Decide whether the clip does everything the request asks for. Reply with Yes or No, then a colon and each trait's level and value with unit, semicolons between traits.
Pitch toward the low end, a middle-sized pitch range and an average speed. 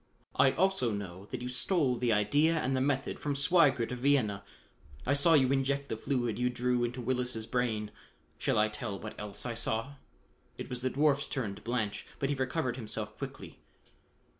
Yes: low, 125 Hz; average, 3.8 semitones; average, 190 wpm